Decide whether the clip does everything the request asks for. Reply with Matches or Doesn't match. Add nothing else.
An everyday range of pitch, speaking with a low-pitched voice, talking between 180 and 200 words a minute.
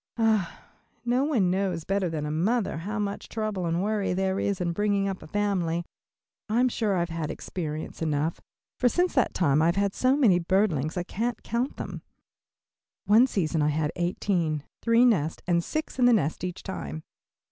Doesn't match